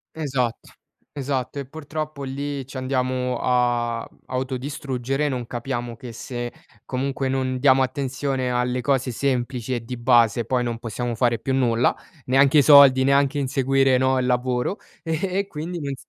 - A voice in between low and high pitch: No, low, 130 Hz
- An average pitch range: No, narrow, 2.0 semitones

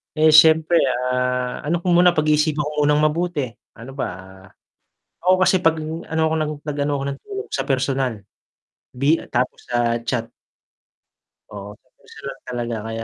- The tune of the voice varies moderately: Yes, average, 4.1 semitones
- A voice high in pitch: No, medium, 150 Hz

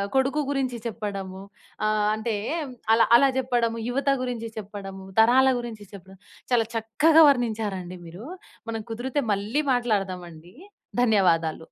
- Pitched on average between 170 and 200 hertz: No, high, 220 Hz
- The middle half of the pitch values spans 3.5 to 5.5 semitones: Yes, average, 4.1 semitones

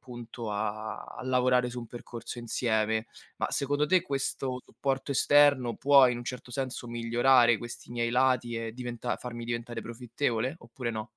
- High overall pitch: No, low, 120 Hz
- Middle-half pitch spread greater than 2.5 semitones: No, narrow, 1.8 semitones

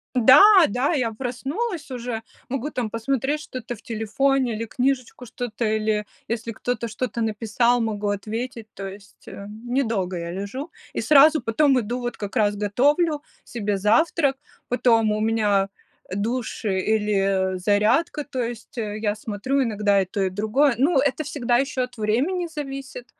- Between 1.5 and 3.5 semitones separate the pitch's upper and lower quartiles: No, average, 4.1 semitones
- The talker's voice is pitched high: Yes, high, 230 Hz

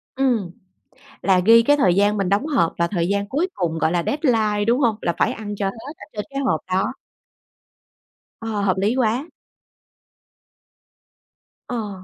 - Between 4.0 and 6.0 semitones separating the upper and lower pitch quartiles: Yes, average, 4.5 semitones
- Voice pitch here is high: Yes, high, 210 Hz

